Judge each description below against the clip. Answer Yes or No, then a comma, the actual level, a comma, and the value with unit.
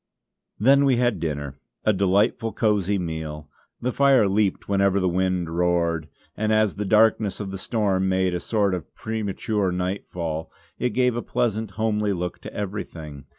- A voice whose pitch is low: Yes, low, 100 Hz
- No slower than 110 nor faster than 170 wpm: Yes, average, 160 wpm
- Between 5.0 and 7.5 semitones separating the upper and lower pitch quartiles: No, average, 3.6 semitones